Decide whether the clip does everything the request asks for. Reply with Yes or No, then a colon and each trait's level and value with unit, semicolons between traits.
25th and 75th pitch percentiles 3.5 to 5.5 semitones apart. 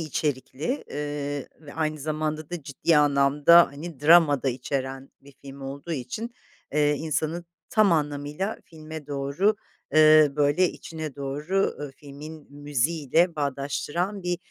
No: narrow, 2.4 semitones